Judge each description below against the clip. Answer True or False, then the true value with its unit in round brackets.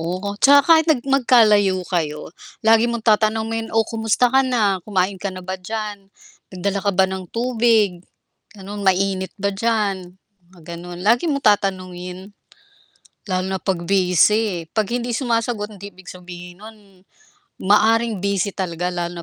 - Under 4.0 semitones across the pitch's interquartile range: True (3.4 semitones)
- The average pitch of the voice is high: True (200 Hz)